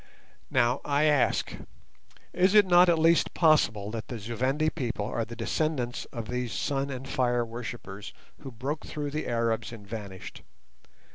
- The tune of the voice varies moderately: Yes, average, 4.6 semitones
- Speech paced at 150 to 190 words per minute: Yes, average, 160 wpm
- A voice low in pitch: Yes, low, 125 Hz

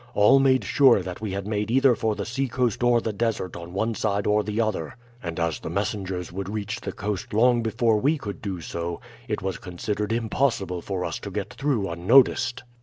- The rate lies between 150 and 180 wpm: No, fast, 205 wpm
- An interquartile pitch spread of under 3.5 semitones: No, average, 3.8 semitones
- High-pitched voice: No, low, 105 Hz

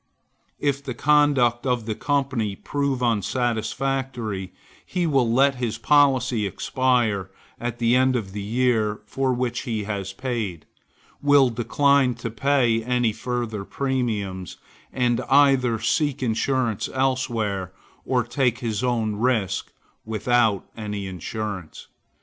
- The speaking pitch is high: No, low, 120 Hz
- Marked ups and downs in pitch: No, average, 3.4 semitones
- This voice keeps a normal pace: No, slow, 120 wpm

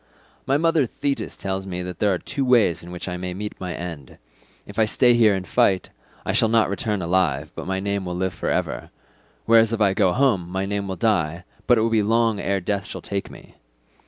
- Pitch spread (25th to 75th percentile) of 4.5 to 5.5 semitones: No, average, 3.8 semitones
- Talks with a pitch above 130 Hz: No, low, 100 Hz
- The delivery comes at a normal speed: No, fast, 230 wpm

